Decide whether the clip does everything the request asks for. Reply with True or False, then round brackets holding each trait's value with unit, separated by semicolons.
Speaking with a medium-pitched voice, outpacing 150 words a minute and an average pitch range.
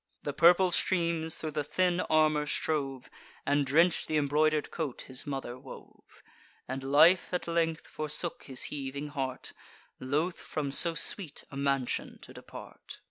False (150 Hz; 145 wpm; 3.1 semitones)